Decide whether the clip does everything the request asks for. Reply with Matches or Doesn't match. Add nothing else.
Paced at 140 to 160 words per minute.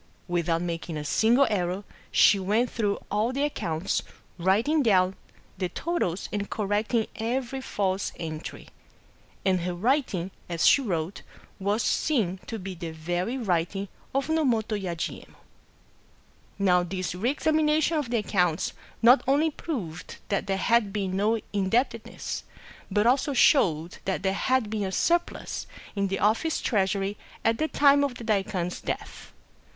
Matches